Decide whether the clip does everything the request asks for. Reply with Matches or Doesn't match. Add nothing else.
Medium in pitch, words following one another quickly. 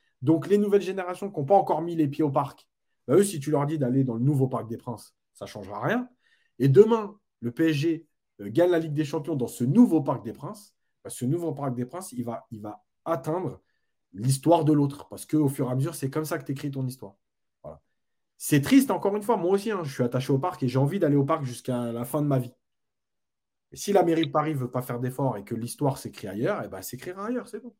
Matches